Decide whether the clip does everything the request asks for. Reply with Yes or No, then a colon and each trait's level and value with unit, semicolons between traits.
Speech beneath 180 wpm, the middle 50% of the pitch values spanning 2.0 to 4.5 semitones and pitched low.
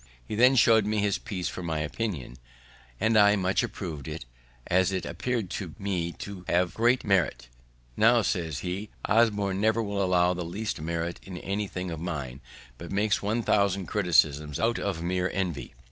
Yes: average, 170 wpm; average, 3.6 semitones; very low, 95 Hz